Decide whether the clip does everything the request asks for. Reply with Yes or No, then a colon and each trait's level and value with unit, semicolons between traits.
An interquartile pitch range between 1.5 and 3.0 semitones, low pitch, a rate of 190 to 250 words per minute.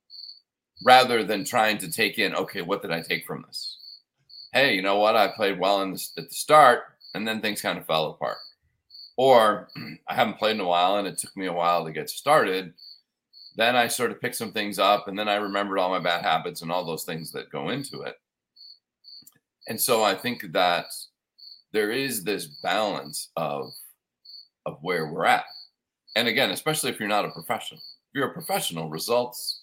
No: average, 4.0 semitones; low, 100 Hz; average, 200 wpm